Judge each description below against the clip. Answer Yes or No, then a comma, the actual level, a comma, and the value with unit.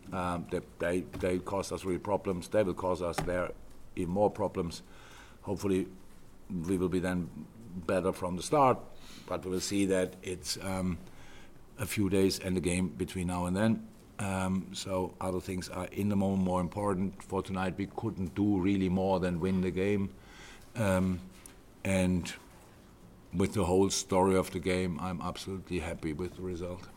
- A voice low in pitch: Yes, very low, 95 Hz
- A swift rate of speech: No, average, 175 wpm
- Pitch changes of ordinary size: No, narrow, 1.1 semitones